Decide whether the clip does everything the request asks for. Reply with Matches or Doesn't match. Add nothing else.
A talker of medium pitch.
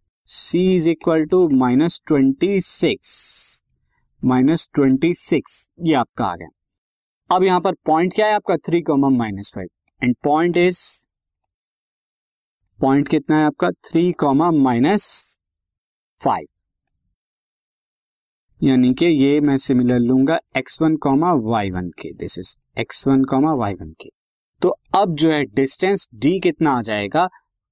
Matches